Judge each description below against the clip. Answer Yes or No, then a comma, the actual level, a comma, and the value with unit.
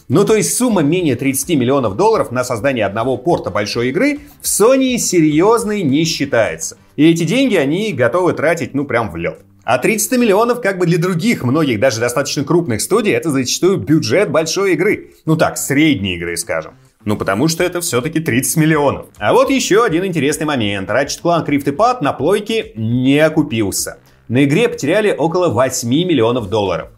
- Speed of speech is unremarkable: No, fast, 175 wpm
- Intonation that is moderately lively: No, wide, 6.4 semitones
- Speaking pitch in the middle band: Yes, medium, 155 Hz